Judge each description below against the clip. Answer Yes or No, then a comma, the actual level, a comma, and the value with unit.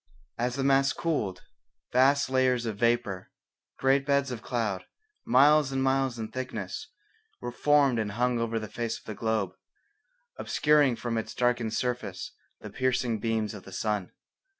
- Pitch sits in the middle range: No, low, 120 Hz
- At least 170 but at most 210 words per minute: No, average, 155 wpm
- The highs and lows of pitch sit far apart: No, average, 3.2 semitones